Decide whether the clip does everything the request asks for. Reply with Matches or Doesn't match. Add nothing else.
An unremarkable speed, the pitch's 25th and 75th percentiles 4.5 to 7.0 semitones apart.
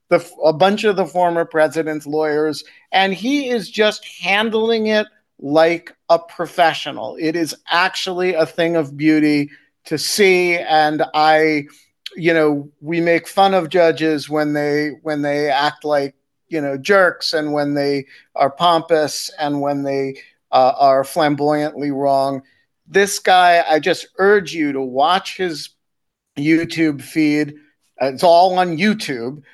Doesn't match